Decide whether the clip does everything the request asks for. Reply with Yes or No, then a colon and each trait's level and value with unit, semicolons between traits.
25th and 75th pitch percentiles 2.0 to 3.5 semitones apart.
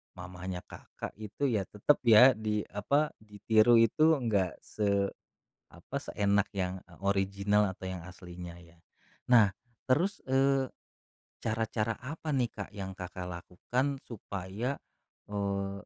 No: average, 4.2 semitones